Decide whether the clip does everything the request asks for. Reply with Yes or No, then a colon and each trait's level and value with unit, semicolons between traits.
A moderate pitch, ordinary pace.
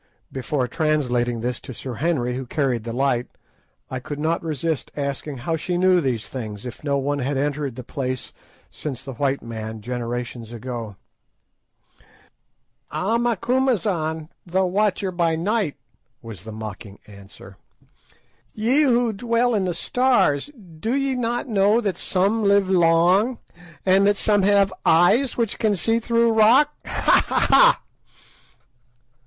Yes: medium, 160 Hz; average, 145 wpm